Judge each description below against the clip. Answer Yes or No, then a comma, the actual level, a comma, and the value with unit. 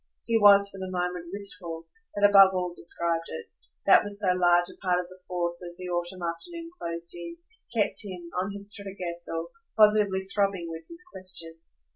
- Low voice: No, medium, 185 Hz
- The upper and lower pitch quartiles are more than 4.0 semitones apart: No, average, 2.7 semitones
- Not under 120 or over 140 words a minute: No, average, 185 wpm